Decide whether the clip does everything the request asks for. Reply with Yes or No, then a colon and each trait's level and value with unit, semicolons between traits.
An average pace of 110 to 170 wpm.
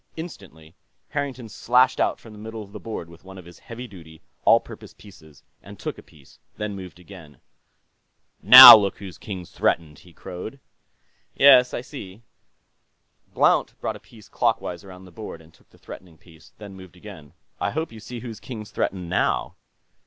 No: average, 180 wpm